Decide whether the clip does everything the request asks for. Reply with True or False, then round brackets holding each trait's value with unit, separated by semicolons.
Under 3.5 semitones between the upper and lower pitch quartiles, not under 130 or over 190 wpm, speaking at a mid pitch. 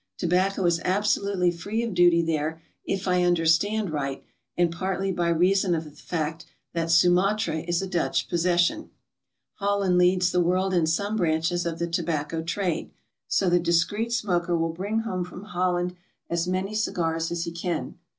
True (2.4 semitones; 165 wpm; 175 Hz)